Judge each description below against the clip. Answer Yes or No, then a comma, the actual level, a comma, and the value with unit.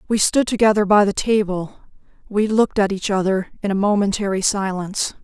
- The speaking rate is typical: Yes, average, 170 wpm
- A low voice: No, high, 200 Hz